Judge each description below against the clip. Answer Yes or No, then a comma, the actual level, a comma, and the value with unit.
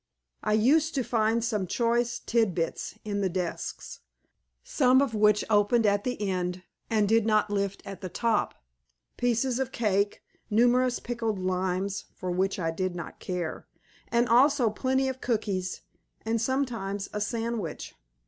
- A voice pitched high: Yes, high, 215 Hz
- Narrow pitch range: No, average, 3.7 semitones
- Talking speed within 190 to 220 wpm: No, average, 150 wpm